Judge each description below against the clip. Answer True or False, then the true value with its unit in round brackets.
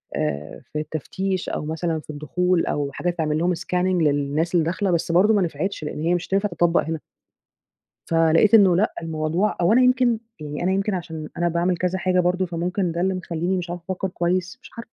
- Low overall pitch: False (175 Hz)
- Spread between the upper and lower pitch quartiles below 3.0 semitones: True (2.6 semitones)